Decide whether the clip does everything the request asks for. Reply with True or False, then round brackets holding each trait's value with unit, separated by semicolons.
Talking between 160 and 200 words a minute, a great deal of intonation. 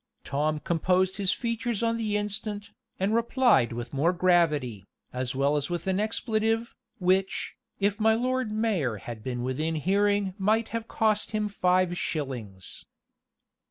False (145 wpm; 6.6 semitones)